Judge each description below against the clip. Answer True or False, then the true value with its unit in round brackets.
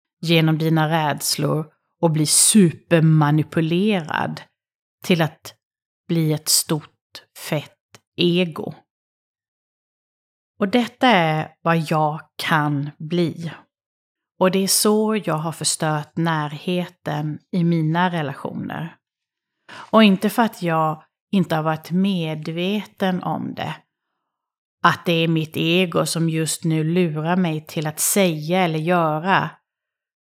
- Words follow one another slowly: True (115 wpm)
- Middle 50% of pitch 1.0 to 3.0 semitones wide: True (2.7 semitones)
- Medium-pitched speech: True (165 Hz)